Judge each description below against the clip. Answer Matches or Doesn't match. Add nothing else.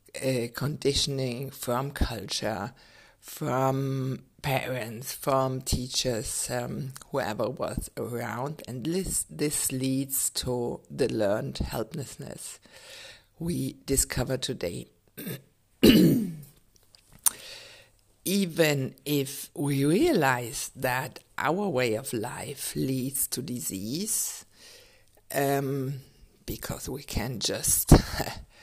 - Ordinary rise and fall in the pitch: Doesn't match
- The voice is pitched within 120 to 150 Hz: Matches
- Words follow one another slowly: Matches